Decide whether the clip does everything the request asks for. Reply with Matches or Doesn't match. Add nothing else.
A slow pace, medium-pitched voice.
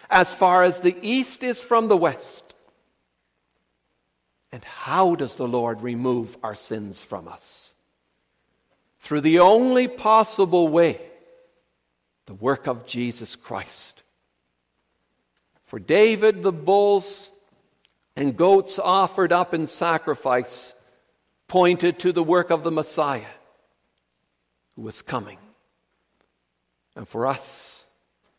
Matches